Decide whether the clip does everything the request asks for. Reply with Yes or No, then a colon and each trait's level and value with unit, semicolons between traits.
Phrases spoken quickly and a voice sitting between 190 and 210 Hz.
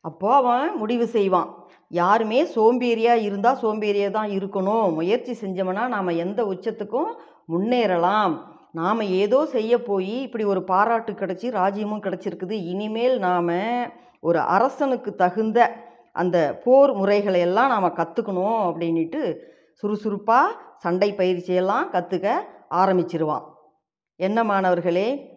No: average, 105 wpm; high, 200 Hz